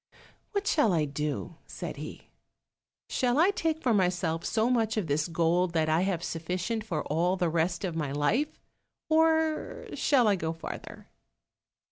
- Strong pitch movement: Yes, wide, 6.9 semitones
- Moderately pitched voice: Yes, medium, 180 Hz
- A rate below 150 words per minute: No, average, 160 wpm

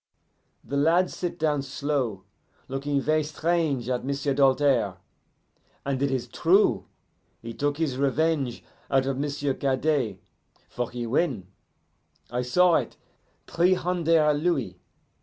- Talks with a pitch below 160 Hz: Yes, medium, 140 Hz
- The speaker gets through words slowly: Yes, slow, 125 wpm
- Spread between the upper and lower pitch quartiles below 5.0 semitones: Yes, average, 3.4 semitones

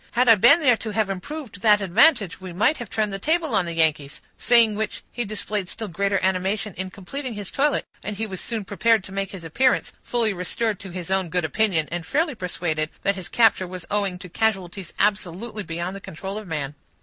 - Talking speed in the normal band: No, fast, 215 wpm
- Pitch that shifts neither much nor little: Yes, average, 3.6 semitones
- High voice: Yes, high, 200 Hz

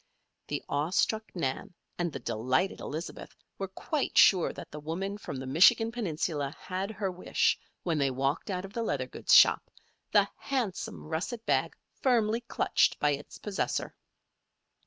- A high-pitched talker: No, medium, 180 Hz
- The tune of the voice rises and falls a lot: Yes, wide, 6.3 semitones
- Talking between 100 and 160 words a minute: Yes, average, 155 wpm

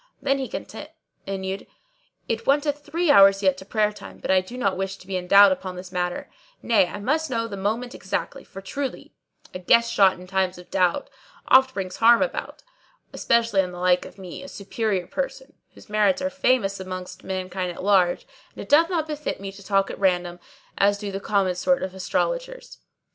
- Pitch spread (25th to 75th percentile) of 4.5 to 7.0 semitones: Yes, average, 5.1 semitones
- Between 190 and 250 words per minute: Yes, average, 200 wpm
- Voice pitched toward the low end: No, high, 200 Hz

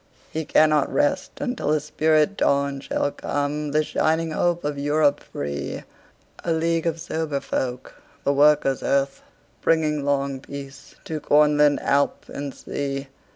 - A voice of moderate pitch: Yes, medium, 150 Hz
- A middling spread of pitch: No, narrow, 2.0 semitones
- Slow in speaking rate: Yes, slow, 120 wpm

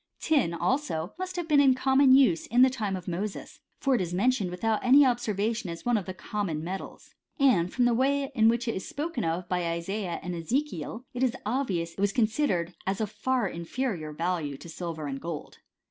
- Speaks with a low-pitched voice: No, high, 210 Hz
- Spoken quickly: Yes, fast, 225 wpm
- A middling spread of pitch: No, wide, 7.0 semitones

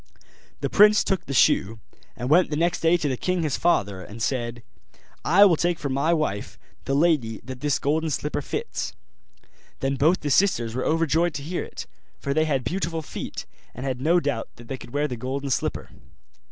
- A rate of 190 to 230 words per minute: Yes, average, 200 wpm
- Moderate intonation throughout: Yes, average, 4.4 semitones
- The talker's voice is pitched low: No, medium, 145 Hz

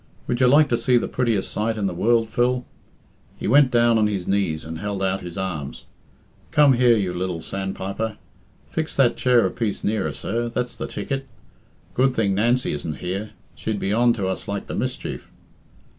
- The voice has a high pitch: No, low, 110 Hz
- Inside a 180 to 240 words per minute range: Yes, average, 190 wpm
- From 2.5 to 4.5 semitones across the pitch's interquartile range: Yes, average, 4.1 semitones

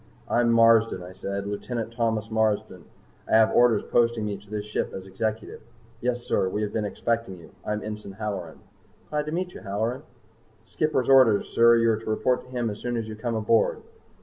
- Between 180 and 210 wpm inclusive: Yes, average, 200 wpm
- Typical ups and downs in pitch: No, narrow, 2.3 semitones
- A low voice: Yes, low, 110 Hz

